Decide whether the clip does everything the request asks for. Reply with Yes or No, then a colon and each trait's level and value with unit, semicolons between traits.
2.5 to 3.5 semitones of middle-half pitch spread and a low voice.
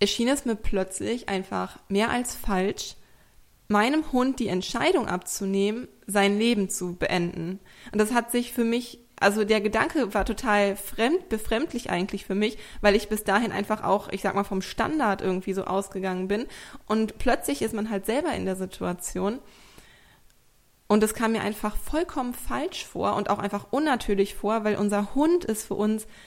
No: average, 3.0 semitones; high, 210 Hz